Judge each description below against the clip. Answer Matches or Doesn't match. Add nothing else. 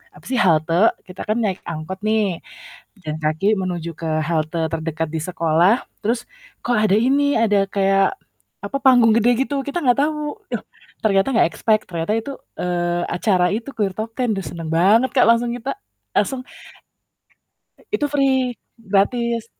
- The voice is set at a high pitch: Matches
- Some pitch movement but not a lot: Doesn't match